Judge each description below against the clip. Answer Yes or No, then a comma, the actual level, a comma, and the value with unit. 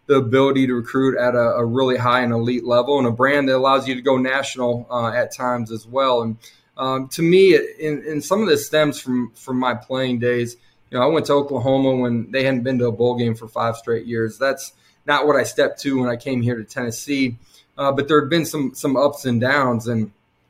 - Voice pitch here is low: Yes, low, 130 Hz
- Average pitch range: No, narrow, 2.2 semitones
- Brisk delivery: Yes, fast, 245 wpm